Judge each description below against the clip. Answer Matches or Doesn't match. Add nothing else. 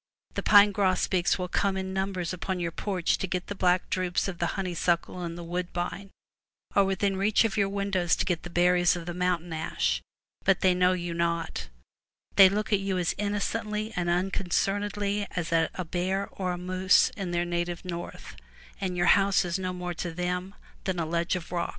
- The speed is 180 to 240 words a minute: Matches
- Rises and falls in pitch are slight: Matches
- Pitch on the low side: Doesn't match